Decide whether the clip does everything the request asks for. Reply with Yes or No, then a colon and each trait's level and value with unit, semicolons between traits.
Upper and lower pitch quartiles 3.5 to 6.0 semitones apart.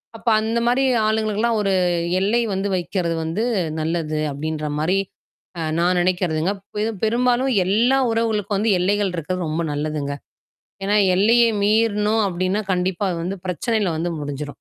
Yes: average, 4.5 semitones